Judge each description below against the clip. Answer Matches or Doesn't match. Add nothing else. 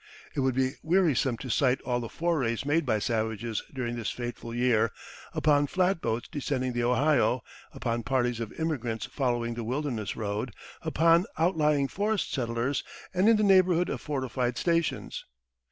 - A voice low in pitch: Matches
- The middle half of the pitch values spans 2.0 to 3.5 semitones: Doesn't match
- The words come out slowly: Doesn't match